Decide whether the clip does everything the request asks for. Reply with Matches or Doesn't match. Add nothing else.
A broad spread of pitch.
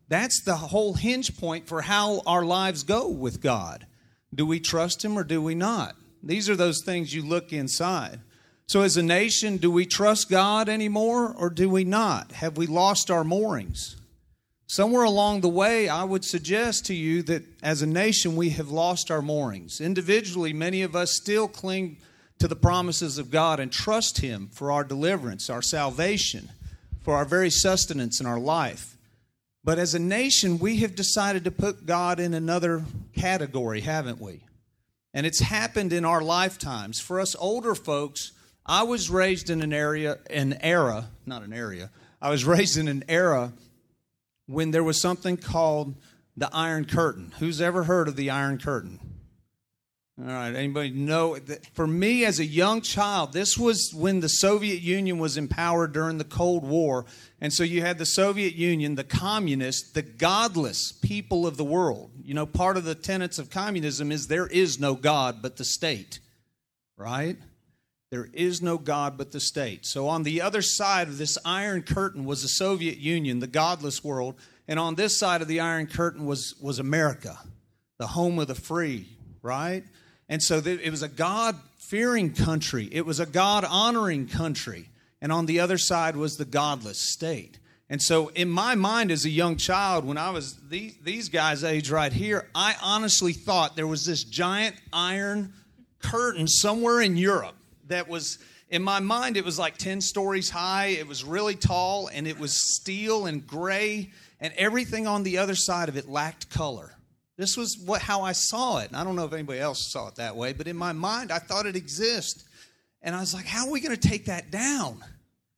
Doesn't match